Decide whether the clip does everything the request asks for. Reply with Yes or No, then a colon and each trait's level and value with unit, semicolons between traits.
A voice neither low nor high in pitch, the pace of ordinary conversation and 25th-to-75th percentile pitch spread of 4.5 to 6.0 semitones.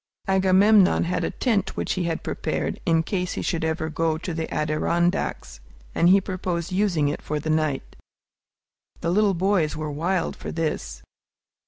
No: medium, 170 Hz; average, 165 wpm; average, 3.0 semitones